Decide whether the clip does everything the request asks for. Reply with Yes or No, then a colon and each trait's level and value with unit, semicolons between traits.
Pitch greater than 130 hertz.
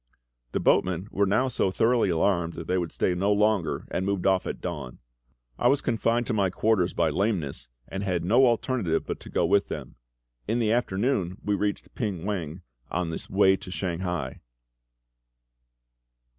No: very low, 95 Hz